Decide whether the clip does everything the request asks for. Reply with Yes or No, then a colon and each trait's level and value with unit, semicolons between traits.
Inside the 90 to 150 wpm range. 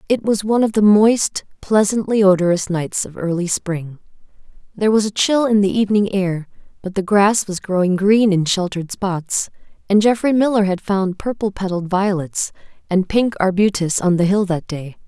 No: average, 180 wpm